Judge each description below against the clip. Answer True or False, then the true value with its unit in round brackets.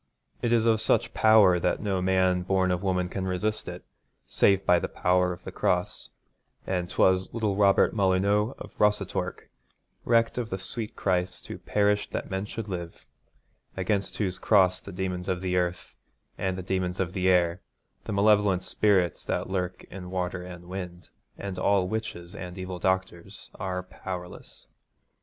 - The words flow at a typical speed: True (160 wpm)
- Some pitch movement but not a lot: False (2.0 semitones)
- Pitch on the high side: False (95 Hz)